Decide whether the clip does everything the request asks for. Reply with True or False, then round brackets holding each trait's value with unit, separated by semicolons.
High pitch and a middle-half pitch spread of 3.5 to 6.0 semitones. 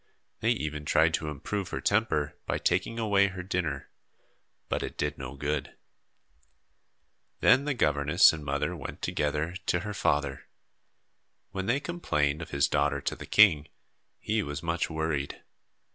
False (80 Hz; 5.1 semitones)